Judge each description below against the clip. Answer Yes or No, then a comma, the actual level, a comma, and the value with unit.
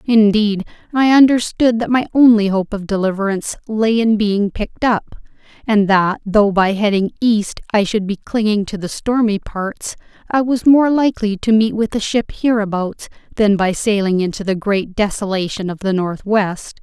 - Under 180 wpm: Yes, average, 170 wpm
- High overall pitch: Yes, high, 210 Hz